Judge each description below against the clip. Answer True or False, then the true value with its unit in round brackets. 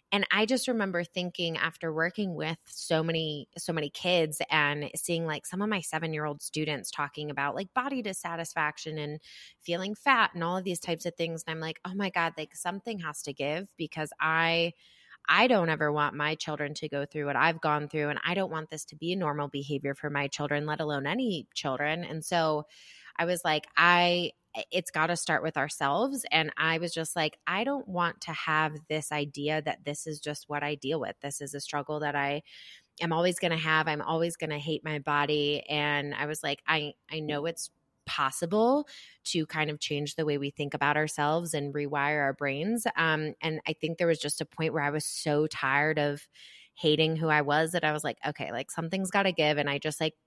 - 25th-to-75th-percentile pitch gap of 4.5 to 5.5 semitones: False (2.4 semitones)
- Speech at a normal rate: False (220 wpm)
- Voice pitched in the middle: True (155 Hz)